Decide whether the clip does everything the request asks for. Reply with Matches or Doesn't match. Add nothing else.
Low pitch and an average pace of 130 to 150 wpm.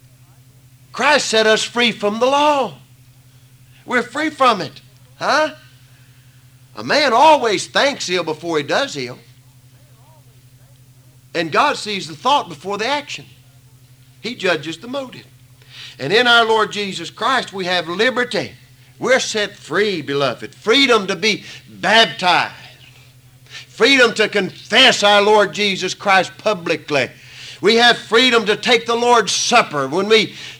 Doesn't match